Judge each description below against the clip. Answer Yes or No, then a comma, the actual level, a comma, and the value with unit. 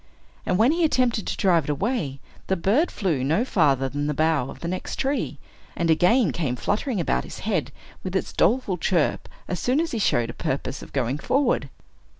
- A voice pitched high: No, medium, 180 Hz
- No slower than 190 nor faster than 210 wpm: Yes, average, 200 wpm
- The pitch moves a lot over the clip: Yes, wide, 8.1 semitones